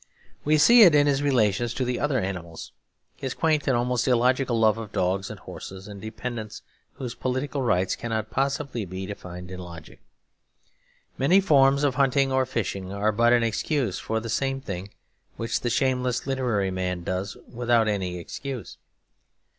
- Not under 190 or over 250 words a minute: No, average, 165 wpm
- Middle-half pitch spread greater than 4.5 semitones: Yes, average, 5.1 semitones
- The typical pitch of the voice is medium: No, low, 120 Hz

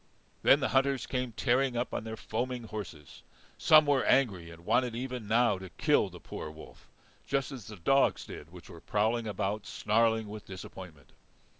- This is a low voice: Yes, low, 110 Hz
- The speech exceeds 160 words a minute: Yes, average, 175 wpm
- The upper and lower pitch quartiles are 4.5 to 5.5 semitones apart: Yes, average, 4.9 semitones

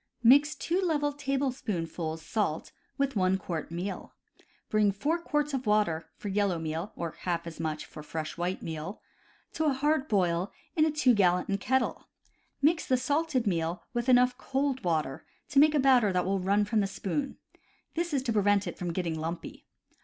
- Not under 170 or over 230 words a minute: Yes, average, 185 wpm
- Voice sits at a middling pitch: No, high, 210 Hz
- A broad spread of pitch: Yes, wide, 7.8 semitones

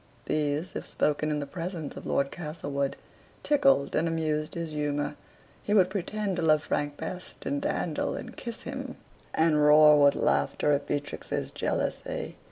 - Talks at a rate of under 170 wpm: Yes, average, 160 wpm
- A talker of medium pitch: Yes, medium, 155 Hz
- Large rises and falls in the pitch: No, average, 3.4 semitones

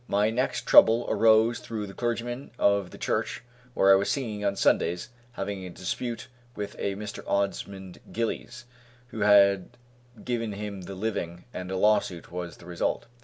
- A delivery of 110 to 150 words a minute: No, average, 165 wpm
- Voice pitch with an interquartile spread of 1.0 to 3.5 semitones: Yes, average, 2.8 semitones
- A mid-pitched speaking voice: No, low, 100 Hz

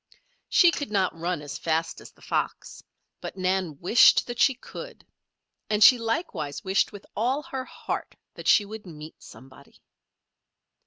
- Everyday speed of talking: Yes, average, 155 wpm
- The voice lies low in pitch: No, high, 200 Hz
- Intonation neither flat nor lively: No, wide, 6.6 semitones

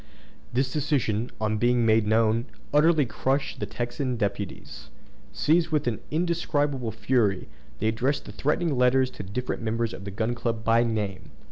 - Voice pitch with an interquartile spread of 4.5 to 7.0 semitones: No, average, 4.0 semitones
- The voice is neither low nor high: No, low, 120 Hz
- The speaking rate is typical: Yes, average, 155 wpm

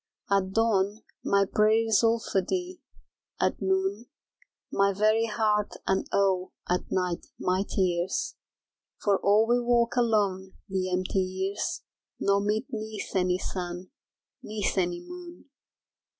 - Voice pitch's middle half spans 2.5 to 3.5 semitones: Yes, average, 2.8 semitones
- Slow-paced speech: Yes, slow, 130 wpm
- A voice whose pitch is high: Yes, high, 200 Hz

